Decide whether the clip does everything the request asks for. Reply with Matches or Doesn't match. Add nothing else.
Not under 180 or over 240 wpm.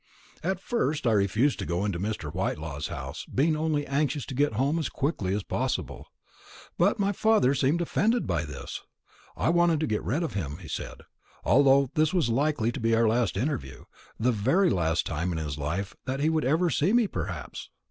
Matches